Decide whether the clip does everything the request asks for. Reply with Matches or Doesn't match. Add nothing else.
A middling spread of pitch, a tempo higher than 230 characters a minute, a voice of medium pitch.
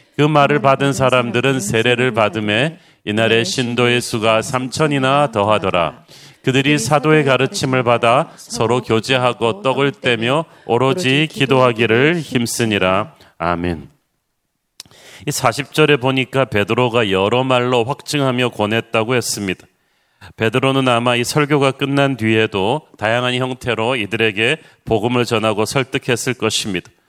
Doesn't match